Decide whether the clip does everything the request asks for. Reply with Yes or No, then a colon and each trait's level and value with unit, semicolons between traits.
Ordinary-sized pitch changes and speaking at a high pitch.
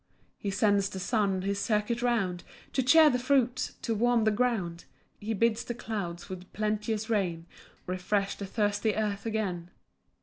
Yes: average, 3.1 semitones; high, 210 Hz